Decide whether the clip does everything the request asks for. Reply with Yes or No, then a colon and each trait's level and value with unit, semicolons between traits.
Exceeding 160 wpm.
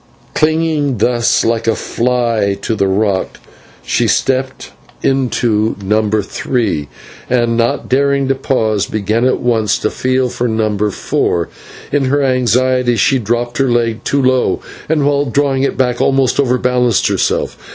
No: average, 145 wpm